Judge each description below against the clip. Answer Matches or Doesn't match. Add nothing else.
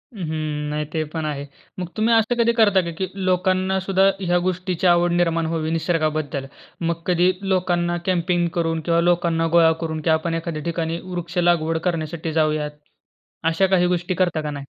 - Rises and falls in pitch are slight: Matches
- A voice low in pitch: Doesn't match